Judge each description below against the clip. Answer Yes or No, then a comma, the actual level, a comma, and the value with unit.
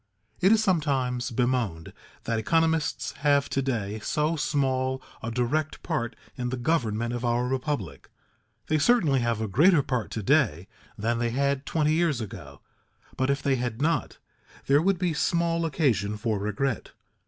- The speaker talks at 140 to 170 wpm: Yes, average, 160 wpm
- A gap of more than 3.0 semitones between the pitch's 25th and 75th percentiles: Yes, average, 4.7 semitones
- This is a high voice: No, low, 130 Hz